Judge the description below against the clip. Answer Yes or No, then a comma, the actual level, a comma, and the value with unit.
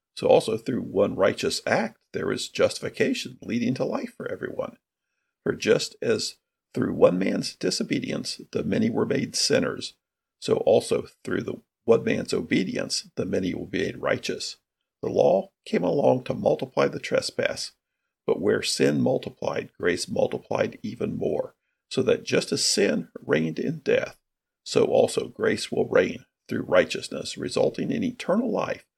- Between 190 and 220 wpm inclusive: No, average, 155 wpm